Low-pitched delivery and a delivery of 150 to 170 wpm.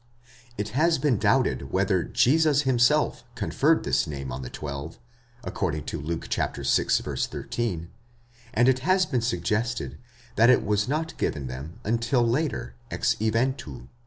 No: low, 115 Hz; average, 140 wpm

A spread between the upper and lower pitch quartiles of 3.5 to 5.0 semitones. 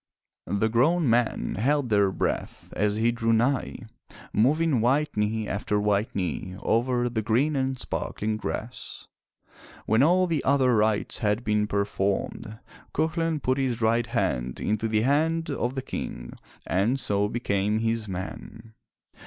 Yes: average, 4.1 semitones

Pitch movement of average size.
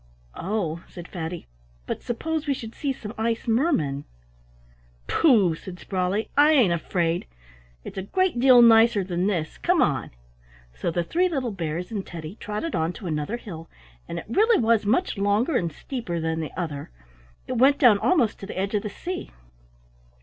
No: wide, 6.3 semitones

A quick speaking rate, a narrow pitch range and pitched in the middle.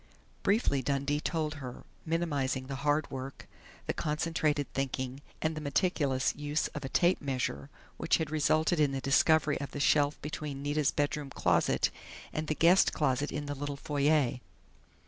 No: average, 160 wpm; narrow, 2.0 semitones; medium, 145 Hz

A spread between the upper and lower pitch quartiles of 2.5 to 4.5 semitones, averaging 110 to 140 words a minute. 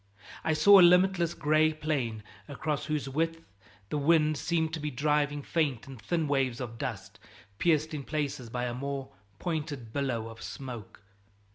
No: average, 3.4 semitones; average, 160 wpm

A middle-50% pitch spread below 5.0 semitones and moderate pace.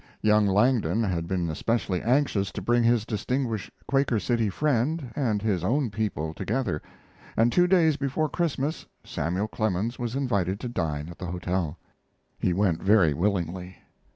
No: wide, 5.6 semitones; average, 155 wpm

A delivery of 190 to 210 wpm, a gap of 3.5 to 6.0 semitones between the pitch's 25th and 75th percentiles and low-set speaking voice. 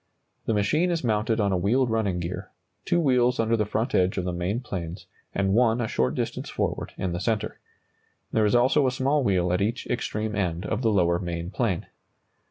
Yes: fast, 205 wpm; average, 4.8 semitones; low, 105 Hz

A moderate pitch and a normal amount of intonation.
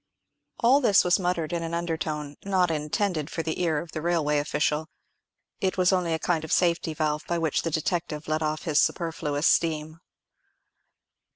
No: medium, 165 Hz; narrow, 2.3 semitones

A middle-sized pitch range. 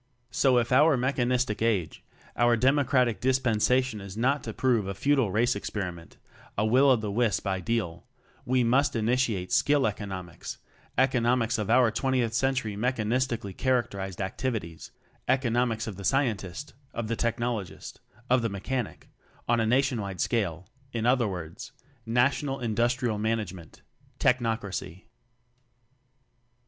Yes: average, 3.7 semitones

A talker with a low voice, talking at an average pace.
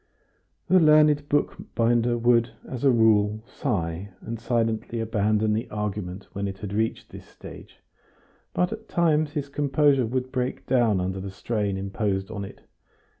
Yes: low, 115 Hz; average, 150 wpm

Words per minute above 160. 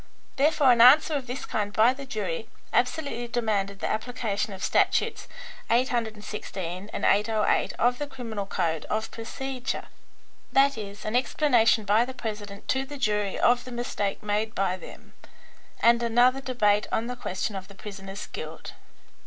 No: average, 155 wpm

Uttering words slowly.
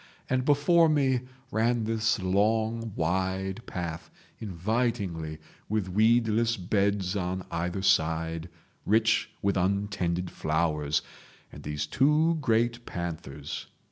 Yes: slow, 105 wpm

